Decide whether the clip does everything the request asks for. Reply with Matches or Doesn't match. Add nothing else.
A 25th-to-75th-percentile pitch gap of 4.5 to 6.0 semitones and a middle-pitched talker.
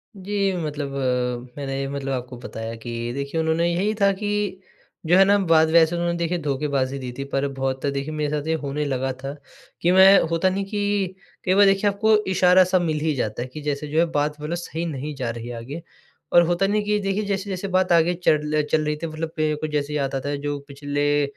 Matches